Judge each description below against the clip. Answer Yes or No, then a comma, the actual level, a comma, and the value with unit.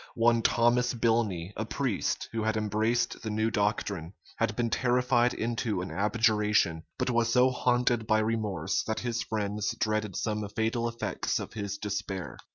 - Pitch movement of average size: No, narrow, 2.1 semitones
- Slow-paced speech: No, average, 160 wpm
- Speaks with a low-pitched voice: Yes, low, 110 Hz